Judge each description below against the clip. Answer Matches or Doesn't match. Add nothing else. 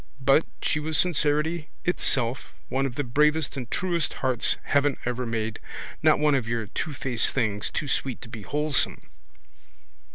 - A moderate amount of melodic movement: Matches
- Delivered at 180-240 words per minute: Doesn't match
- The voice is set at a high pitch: Doesn't match